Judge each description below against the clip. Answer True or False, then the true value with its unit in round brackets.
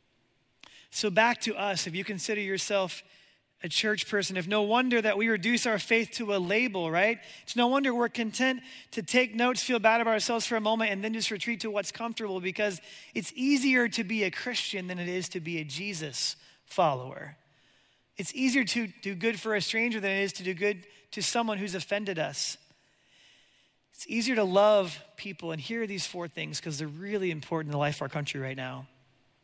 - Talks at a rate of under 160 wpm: False (205 wpm)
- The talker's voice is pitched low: False (205 Hz)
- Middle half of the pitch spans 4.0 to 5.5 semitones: True (4.5 semitones)